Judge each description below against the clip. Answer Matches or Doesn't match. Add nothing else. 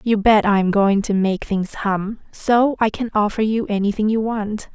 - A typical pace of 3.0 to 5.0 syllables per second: Matches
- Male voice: Doesn't match